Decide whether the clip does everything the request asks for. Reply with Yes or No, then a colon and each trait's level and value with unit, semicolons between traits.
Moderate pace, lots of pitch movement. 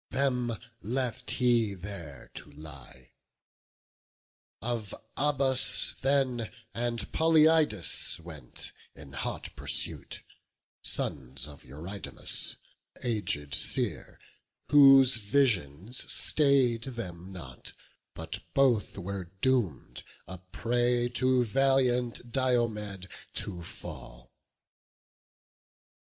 No: slow, 85 wpm; wide, 6.5 semitones